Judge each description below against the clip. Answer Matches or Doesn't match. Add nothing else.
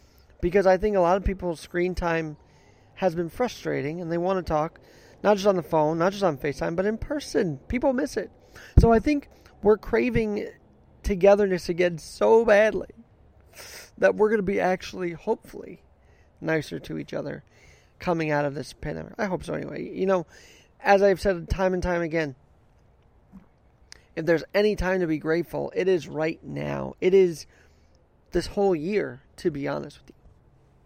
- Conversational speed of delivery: Matches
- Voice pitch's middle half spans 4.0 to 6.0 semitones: Matches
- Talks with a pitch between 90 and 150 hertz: Doesn't match